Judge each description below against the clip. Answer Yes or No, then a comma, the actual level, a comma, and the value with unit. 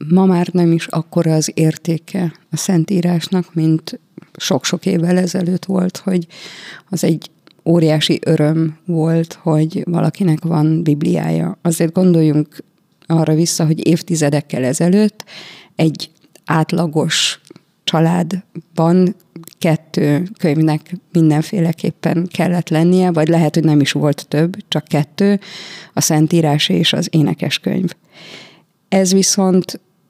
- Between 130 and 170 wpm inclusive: No, average, 110 wpm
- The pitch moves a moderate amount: No, narrow, 2.3 semitones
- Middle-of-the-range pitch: Yes, medium, 170 Hz